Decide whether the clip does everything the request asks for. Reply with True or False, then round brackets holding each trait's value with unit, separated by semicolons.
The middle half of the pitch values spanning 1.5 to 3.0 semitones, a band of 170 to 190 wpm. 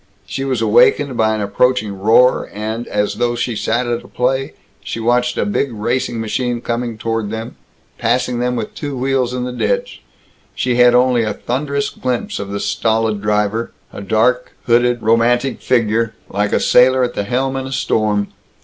True (2.5 semitones; 180 wpm)